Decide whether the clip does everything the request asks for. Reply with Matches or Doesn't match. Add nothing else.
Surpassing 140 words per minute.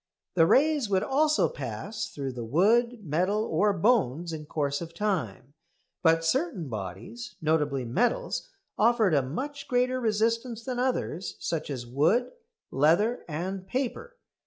Doesn't match